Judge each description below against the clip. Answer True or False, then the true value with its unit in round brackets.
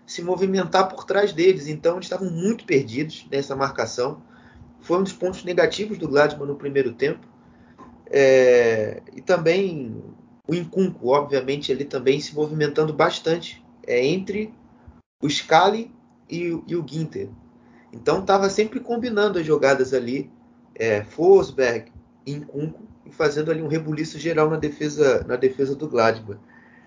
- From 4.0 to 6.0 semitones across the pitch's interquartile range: True (5.4 semitones)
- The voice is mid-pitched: True (155 Hz)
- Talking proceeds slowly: False (145 wpm)